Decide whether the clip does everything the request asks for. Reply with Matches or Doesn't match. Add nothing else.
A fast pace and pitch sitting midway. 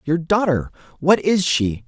Doesn't match